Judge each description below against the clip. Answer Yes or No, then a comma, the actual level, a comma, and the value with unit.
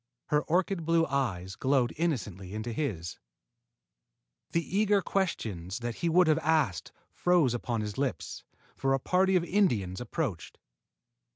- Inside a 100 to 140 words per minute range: Yes, slow, 135 wpm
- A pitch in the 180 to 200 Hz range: No, low, 135 Hz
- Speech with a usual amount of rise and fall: No, wide, 7.8 semitones